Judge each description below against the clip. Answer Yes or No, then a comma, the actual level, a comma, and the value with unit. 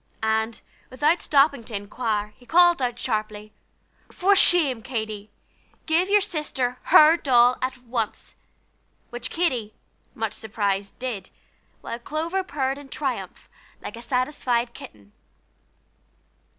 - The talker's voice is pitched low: No, very high, 250 Hz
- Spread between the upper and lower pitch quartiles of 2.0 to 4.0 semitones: No, average, 5.1 semitones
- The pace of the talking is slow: Yes, slow, 120 wpm